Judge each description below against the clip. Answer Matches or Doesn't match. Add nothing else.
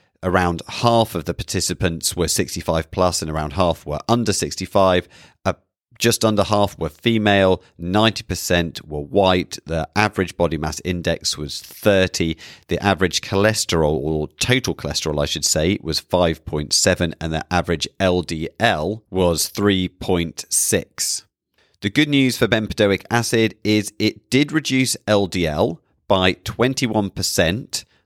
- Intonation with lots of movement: Doesn't match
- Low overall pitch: Matches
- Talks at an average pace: Doesn't match